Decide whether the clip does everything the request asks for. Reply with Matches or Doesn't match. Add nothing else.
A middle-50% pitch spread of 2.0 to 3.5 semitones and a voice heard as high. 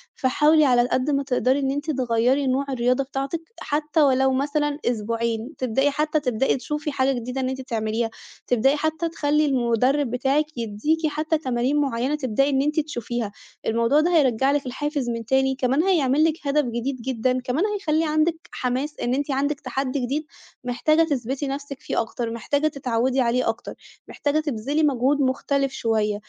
Matches